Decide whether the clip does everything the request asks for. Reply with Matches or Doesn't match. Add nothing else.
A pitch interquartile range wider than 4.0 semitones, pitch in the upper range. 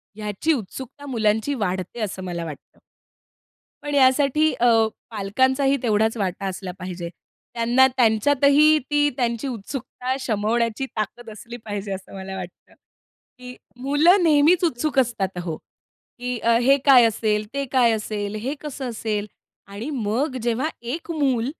Matches